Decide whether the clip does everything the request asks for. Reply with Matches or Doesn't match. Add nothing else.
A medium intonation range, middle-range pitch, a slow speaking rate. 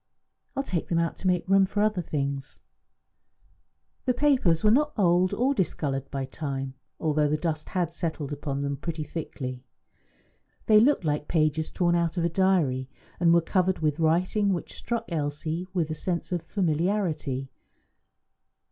Doesn't match